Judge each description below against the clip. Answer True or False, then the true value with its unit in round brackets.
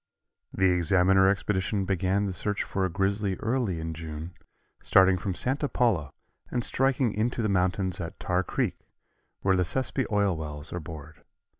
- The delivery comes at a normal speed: True (160 wpm)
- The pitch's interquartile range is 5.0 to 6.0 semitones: False (3.0 semitones)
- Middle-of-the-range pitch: False (95 Hz)